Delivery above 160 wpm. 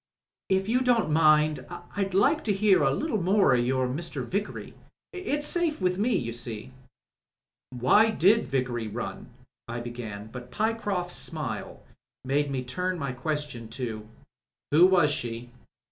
No: average, 145 wpm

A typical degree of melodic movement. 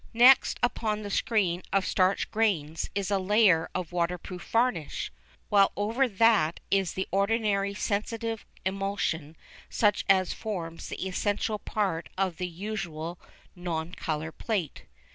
Yes: average, 3.5 semitones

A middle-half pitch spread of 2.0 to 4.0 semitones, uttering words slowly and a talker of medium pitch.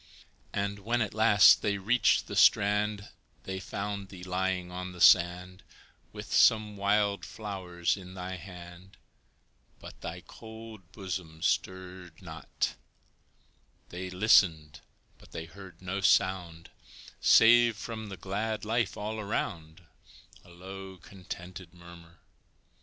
No: narrow, 2.6 semitones; slow, 120 wpm; very low, 95 Hz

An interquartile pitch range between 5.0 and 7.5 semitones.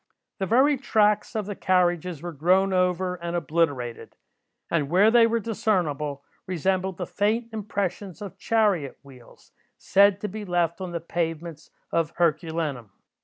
No: average, 3.9 semitones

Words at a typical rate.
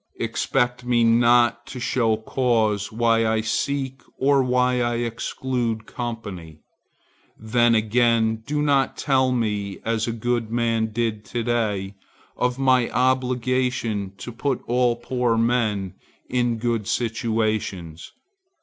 No: slow, 120 wpm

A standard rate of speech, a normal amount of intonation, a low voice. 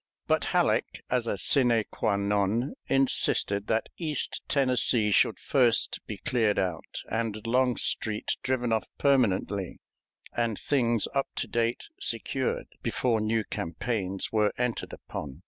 No: slow, 130 wpm; average, 3.4 semitones; low, 115 Hz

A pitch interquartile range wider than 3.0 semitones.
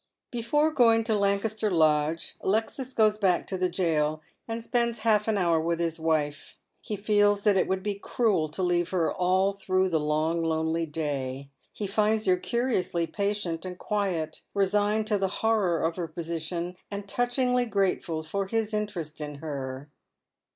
Yes: average, 4.5 semitones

